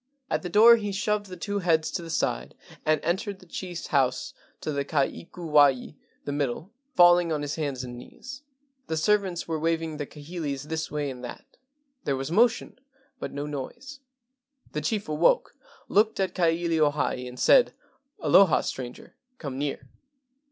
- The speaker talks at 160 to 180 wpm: Yes, average, 170 wpm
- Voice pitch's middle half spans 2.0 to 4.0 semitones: No, average, 4.8 semitones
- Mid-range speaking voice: Yes, medium, 160 Hz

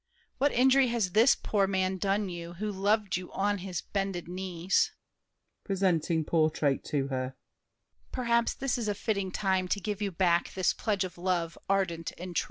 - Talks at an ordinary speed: Yes, average, 175 wpm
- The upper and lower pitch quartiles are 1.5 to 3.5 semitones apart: Yes, average, 3.0 semitones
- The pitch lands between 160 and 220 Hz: Yes, high, 190 Hz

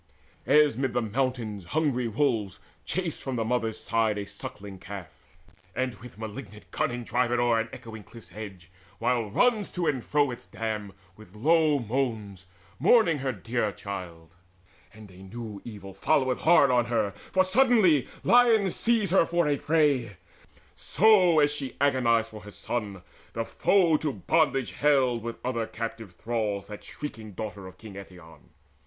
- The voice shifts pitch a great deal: Yes, wide, 5.8 semitones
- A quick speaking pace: No, average, 160 wpm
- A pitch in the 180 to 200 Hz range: No, low, 120 Hz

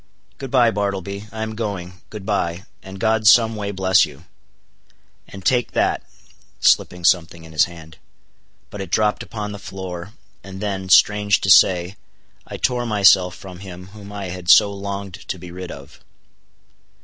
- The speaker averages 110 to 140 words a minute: No, average, 155 wpm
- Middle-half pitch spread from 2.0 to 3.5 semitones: Yes, narrow, 2.4 semitones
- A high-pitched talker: No, low, 100 Hz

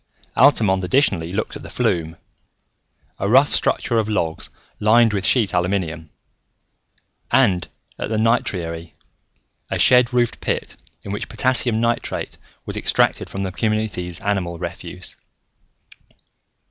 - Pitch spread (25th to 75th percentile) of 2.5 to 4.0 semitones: No, average, 4.9 semitones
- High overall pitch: No, low, 100 Hz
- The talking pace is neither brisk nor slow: No, slow, 120 wpm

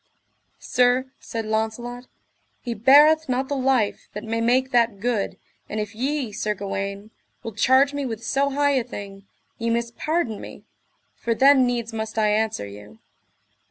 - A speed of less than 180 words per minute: Yes, average, 160 wpm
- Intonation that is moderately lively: Yes, average, 3.5 semitones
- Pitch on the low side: No, high, 235 Hz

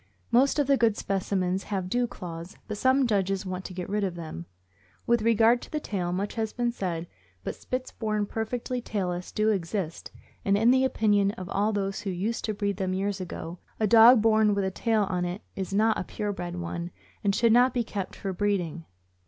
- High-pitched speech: Yes, high, 205 Hz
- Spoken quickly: Yes, fast, 210 wpm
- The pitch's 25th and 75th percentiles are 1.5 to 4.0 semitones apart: Yes, average, 3.3 semitones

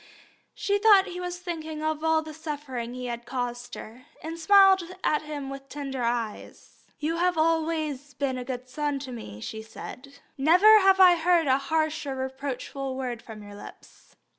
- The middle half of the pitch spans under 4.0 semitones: No, average, 4.3 semitones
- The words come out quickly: No, average, 180 wpm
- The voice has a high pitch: Yes, very high, 290 Hz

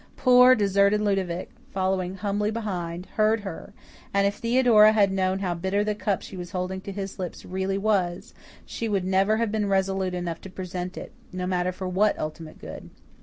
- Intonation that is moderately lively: No, narrow, 2.3 semitones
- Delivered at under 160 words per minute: No, average, 185 wpm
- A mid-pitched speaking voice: No, high, 195 Hz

